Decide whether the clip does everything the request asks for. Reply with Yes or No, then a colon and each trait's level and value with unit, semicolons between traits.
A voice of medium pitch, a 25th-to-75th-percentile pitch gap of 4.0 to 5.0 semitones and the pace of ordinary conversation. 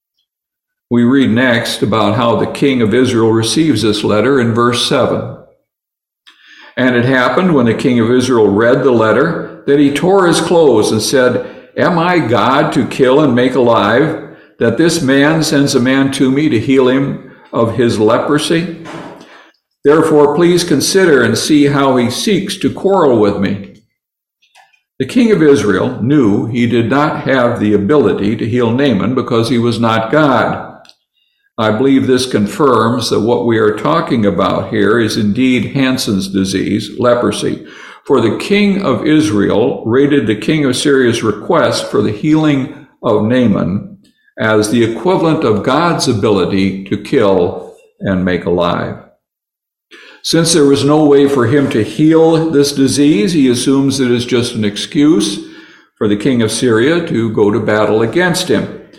No: low, 130 Hz; average, 4.7 semitones; average, 160 wpm